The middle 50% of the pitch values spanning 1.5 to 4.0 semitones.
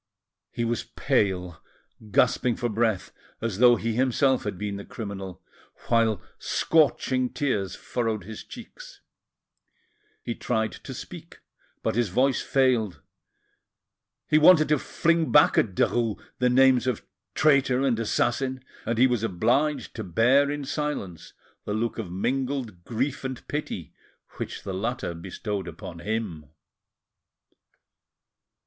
No: average, 4.4 semitones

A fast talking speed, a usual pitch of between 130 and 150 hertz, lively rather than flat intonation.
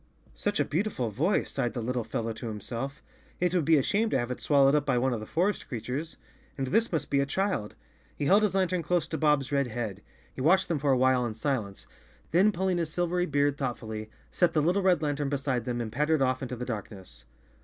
Yes: fast, 240 wpm; medium, 140 Hz; wide, 5.8 semitones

